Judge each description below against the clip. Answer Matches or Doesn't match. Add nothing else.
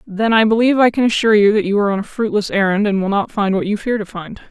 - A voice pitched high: Matches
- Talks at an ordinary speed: Doesn't match